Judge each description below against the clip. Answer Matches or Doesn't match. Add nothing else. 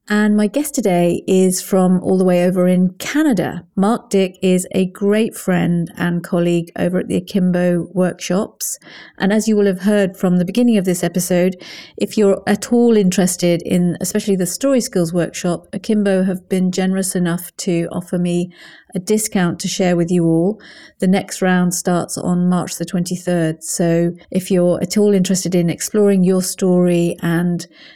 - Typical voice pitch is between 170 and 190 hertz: Matches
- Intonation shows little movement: Matches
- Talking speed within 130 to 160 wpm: Doesn't match